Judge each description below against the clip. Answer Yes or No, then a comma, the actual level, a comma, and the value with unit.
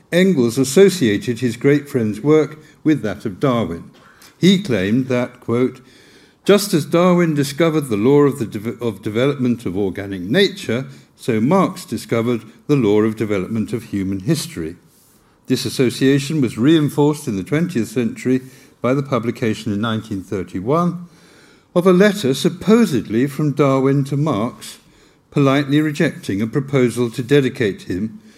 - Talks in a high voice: No, low, 135 Hz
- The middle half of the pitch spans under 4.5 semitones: No, average, 5.1 semitones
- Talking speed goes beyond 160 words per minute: No, average, 140 wpm